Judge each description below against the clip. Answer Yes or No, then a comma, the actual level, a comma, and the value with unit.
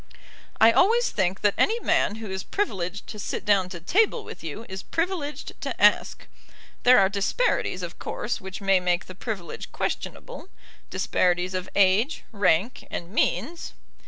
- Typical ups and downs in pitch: No, wide, 7.9 semitones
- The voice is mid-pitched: No, high, 200 Hz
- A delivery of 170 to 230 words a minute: No, average, 160 wpm